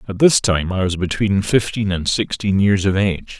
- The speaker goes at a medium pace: No, fast, 210 wpm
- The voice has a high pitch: No, low, 100 Hz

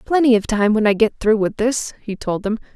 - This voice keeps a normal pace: No, fast, 260 wpm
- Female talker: Yes, female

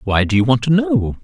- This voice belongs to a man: Yes, male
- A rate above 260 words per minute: Yes, fast, 290 wpm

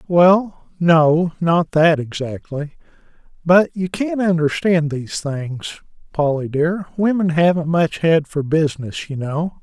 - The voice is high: No, medium, 165 Hz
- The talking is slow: Yes, slow, 120 wpm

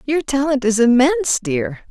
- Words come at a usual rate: Yes, average, 155 wpm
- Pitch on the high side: Yes, very high, 260 Hz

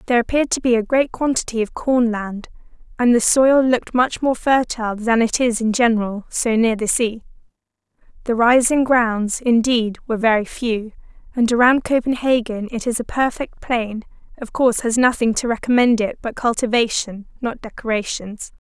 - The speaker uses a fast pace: No, average, 165 wpm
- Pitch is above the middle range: Yes, high, 235 Hz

